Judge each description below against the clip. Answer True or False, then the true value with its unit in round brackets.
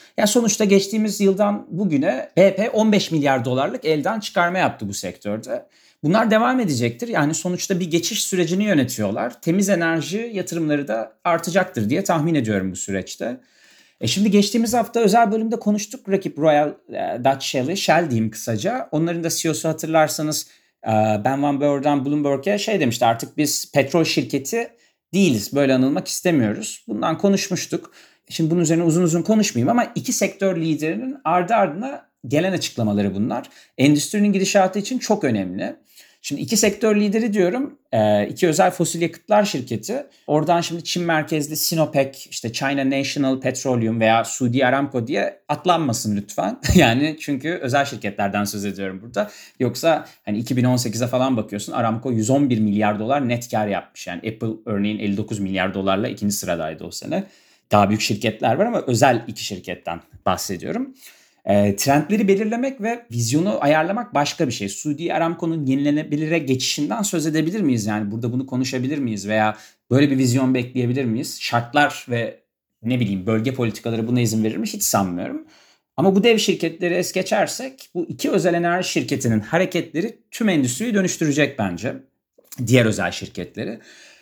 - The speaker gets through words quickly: True (150 wpm)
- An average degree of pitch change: False (8.3 semitones)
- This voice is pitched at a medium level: True (150 Hz)